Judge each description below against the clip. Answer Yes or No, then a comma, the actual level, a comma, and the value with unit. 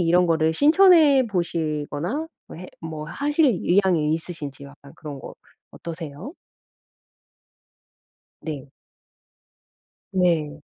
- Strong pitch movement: No, average, 4.7 semitones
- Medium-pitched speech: Yes, medium, 165 Hz